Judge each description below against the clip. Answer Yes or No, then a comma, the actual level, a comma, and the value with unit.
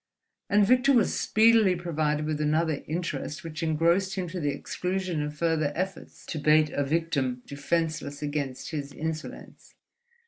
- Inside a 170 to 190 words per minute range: No, average, 145 wpm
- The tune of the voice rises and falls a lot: No, average, 3.3 semitones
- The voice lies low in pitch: No, medium, 160 Hz